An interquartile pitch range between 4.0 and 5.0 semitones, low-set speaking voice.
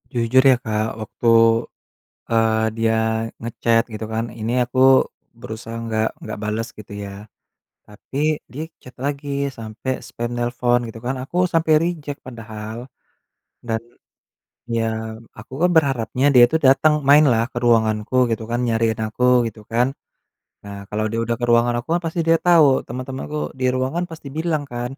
No: average, 3.3 semitones; low, 120 Hz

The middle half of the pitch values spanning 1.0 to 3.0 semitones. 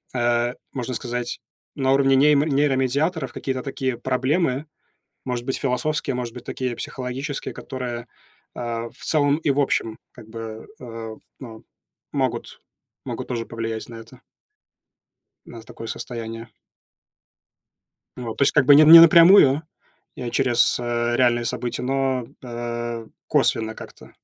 Yes: narrow, 2.5 semitones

